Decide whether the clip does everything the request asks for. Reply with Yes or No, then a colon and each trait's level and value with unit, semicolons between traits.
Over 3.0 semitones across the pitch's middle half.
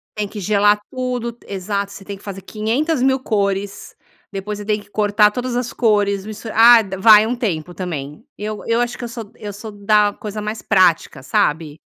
No: narrow, 2.4 semitones